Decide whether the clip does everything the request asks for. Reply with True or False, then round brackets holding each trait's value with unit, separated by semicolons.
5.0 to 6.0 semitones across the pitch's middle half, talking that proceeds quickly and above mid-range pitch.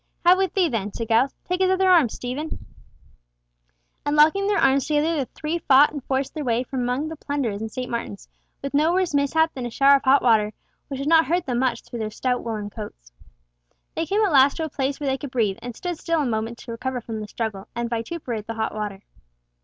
True (5.3 semitones; 235 wpm; 260 Hz)